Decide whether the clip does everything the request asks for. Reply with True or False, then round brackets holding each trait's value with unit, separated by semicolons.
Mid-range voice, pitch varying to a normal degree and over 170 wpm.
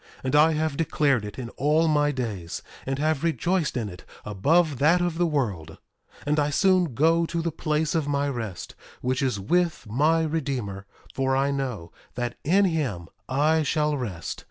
True (145 Hz; 4.6 semitones; 180 wpm)